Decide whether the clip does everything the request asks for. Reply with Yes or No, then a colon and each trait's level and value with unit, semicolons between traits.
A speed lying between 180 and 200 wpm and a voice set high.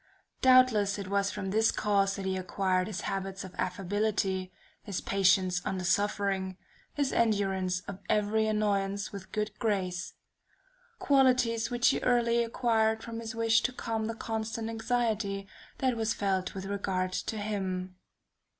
No: average, 150 wpm; high, 205 Hz